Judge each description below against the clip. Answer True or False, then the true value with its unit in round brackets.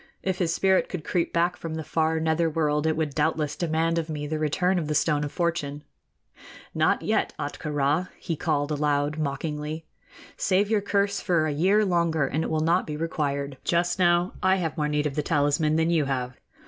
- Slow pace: False (205 wpm)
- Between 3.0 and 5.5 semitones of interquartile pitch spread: False (2.5 semitones)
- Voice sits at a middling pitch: True (160 Hz)